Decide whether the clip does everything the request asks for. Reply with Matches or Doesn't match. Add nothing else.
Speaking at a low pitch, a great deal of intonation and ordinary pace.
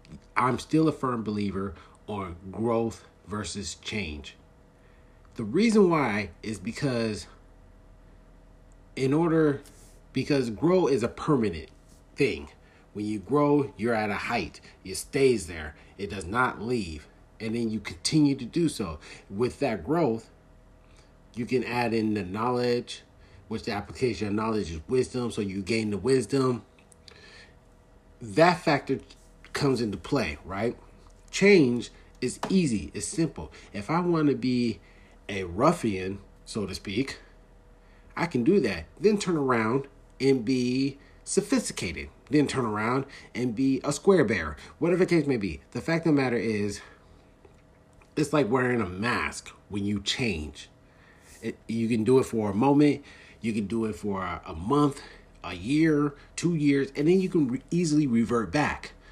Matches